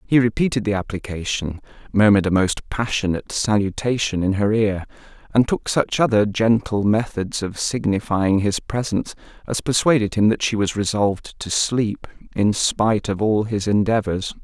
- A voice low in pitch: Yes, low, 105 Hz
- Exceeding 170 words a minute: No, average, 155 wpm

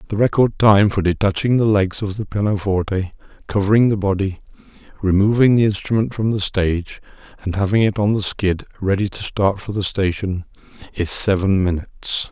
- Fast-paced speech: No, average, 165 wpm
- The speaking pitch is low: Yes, low, 100 Hz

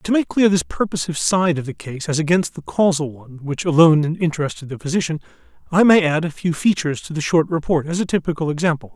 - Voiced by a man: Yes, male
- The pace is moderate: No, fast, 220 wpm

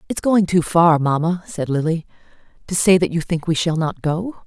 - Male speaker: No, female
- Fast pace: Yes, fast, 215 wpm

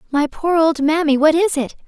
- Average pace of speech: No, fast, 225 wpm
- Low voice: No, very high, 305 Hz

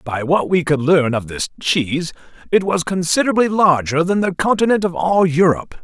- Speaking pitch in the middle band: Yes, medium, 170 Hz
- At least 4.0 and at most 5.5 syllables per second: Yes, 5.3 syllables/s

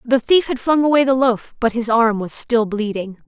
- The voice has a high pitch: Yes, high, 240 Hz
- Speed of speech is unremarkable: No, fast, 240 wpm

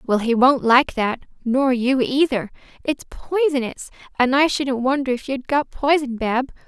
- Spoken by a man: No, female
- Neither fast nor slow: Yes, average, 170 wpm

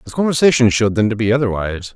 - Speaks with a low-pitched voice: Yes, low, 115 Hz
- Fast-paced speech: Yes, fast, 215 wpm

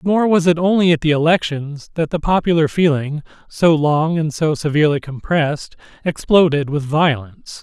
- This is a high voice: No, medium, 155 Hz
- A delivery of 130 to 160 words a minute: Yes, average, 155 wpm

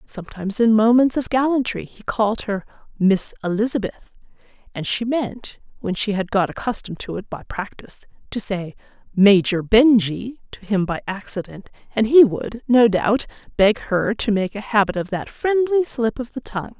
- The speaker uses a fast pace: No, average, 170 wpm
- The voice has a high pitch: Yes, high, 220 Hz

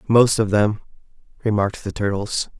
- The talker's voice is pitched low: Yes, low, 105 Hz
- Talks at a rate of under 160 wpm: Yes, average, 140 wpm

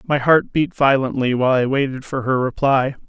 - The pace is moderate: Yes, average, 195 wpm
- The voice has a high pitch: No, low, 135 Hz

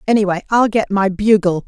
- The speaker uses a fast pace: No, average, 180 wpm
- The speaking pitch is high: Yes, high, 200 Hz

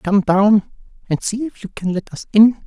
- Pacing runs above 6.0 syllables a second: No, 4.5 syllables/s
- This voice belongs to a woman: No, male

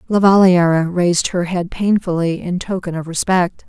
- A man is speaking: No, female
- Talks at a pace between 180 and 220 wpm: No, average, 165 wpm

